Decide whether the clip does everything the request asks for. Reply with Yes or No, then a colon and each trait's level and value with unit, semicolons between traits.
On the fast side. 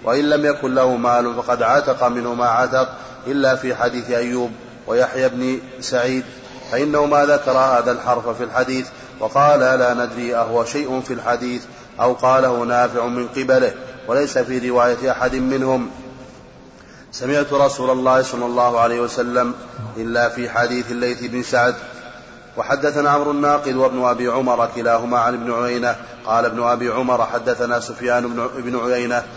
Yes: fast, 145 wpm